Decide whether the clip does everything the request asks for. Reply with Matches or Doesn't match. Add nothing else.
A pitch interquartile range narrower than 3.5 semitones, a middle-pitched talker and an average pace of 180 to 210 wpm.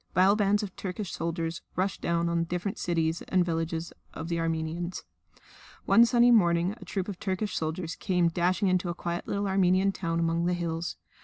Matches